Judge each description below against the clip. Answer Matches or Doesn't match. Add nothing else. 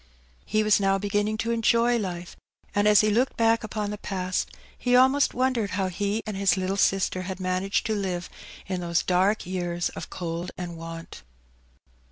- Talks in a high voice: Matches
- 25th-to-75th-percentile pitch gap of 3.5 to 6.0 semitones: Doesn't match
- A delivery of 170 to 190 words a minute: Matches